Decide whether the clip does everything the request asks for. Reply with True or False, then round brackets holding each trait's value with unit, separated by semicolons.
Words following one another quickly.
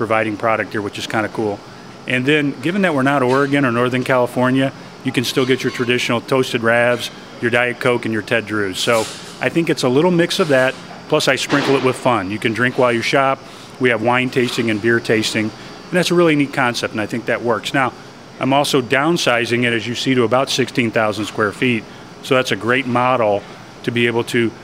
True (230 wpm)